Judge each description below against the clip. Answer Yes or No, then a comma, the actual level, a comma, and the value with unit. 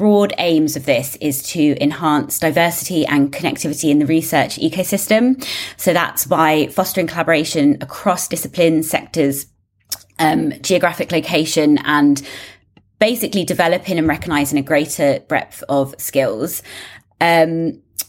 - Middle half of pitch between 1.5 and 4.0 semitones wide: Yes, average, 3.2 semitones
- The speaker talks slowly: Yes, slow, 120 wpm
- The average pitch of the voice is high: No, medium, 160 Hz